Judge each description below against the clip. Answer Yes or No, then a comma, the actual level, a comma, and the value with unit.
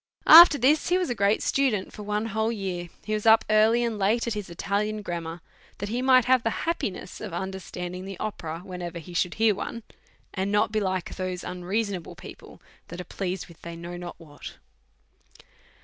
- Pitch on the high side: Yes, high, 200 Hz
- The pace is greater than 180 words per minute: Yes, average, 195 wpm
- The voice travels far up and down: No, average, 3.9 semitones